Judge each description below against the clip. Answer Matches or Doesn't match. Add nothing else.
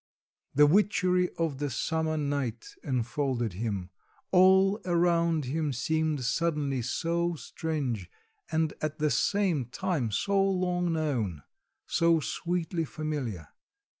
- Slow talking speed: Matches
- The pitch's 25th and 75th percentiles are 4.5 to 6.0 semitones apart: Matches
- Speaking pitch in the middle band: Matches